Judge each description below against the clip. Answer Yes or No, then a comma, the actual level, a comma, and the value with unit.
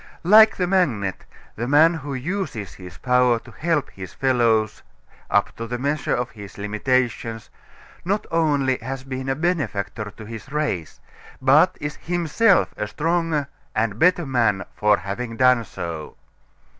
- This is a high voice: No, low, 130 Hz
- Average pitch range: No, wide, 6.3 semitones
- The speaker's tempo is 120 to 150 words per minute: Yes, average, 145 wpm